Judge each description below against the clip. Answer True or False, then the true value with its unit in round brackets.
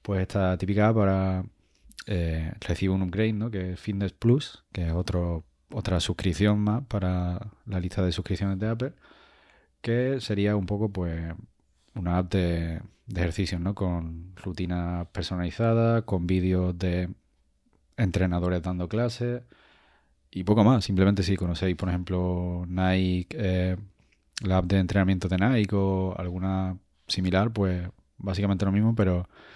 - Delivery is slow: False (140 wpm)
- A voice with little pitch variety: True (2.3 semitones)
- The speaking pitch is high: False (95 Hz)